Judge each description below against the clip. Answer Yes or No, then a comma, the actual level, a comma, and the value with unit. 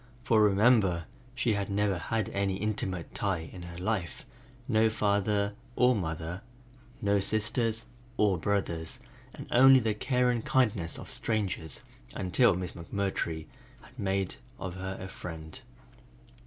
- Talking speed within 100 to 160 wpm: Yes, slow, 135 wpm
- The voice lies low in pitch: Yes, low, 100 Hz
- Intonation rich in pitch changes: No, average, 3.5 semitones